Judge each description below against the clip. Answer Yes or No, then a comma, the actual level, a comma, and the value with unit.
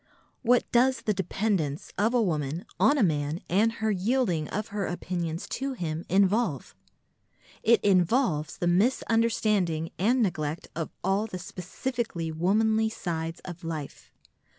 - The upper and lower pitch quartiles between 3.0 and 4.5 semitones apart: No, average, 5.3 semitones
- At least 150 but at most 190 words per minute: No, slow, 135 wpm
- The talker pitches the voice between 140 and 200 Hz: Yes, high, 190 Hz